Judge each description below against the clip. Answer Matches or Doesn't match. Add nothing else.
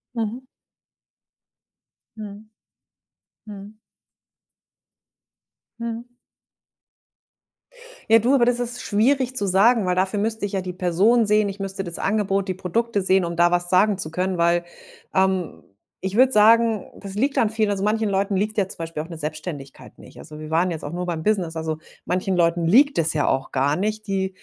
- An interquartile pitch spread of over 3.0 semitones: Matches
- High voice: Matches